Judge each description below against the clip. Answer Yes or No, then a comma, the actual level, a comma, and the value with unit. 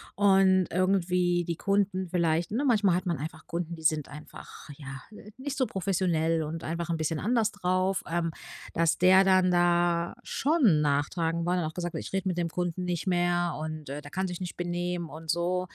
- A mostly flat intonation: Yes, narrow, 2.3 semitones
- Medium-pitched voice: Yes, medium, 175 Hz